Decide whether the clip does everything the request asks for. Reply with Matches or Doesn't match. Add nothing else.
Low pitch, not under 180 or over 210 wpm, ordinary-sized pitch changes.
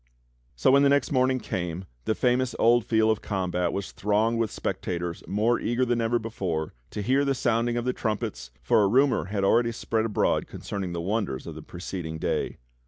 Matches